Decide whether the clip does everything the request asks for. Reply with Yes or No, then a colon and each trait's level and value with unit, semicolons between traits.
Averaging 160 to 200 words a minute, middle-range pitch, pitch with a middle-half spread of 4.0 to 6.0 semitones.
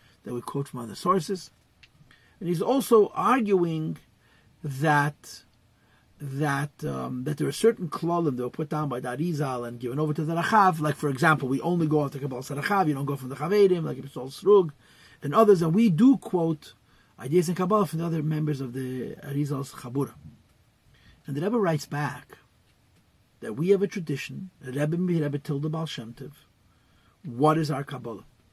Yes: average, 185 wpm; medium, 150 Hz; average, 5.0 semitones